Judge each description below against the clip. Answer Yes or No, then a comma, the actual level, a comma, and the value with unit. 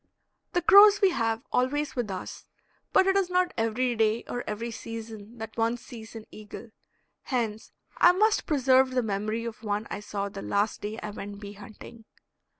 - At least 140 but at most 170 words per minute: No, average, 180 wpm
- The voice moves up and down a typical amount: Yes, average, 3.4 semitones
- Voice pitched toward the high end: Yes, high, 225 Hz